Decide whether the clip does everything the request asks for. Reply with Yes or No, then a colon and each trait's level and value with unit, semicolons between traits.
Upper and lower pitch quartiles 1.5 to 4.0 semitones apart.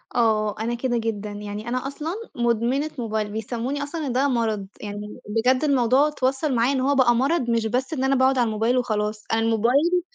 Yes: average, 3.3 semitones